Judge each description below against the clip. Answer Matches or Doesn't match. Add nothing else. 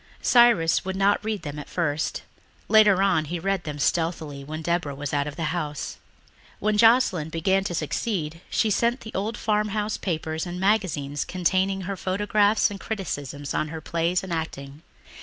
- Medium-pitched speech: Matches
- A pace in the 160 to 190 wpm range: Matches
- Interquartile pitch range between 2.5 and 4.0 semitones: Doesn't match